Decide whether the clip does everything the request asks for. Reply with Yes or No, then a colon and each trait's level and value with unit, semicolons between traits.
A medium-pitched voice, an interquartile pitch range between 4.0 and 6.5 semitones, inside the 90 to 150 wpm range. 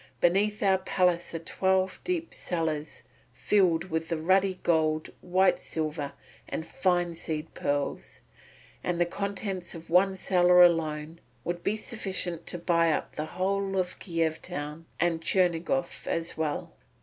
No: medium, 175 Hz; narrow, 2.6 semitones; slow, 135 wpm